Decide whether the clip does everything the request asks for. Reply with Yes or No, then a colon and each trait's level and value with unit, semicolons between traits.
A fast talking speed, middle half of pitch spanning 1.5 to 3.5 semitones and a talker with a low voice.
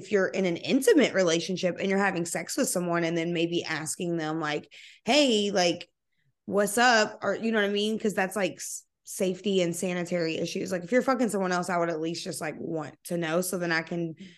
No: fast, 225 wpm; average, 2.9 semitones; medium, 180 Hz